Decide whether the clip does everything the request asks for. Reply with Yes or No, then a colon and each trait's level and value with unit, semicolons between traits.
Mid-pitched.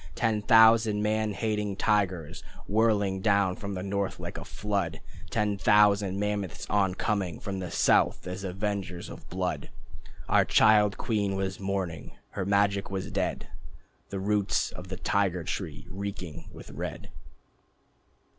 No: low, 100 Hz